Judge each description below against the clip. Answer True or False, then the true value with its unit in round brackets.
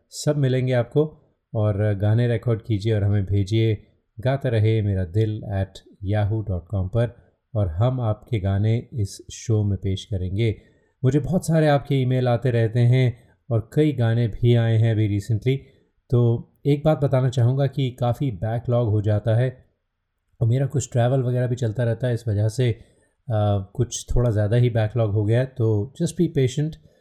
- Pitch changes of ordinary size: True (3.2 semitones)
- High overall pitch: False (115 Hz)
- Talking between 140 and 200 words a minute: True (175 wpm)